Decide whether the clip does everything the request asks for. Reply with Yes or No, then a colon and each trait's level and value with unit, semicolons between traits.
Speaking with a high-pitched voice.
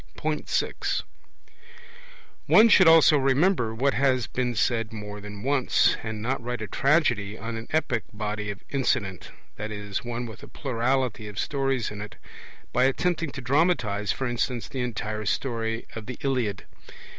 No: low, 120 Hz